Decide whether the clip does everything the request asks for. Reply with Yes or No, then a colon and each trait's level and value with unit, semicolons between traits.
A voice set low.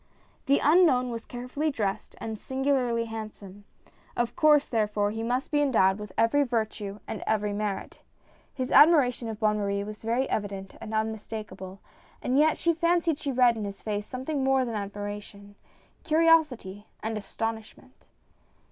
No: high, 225 Hz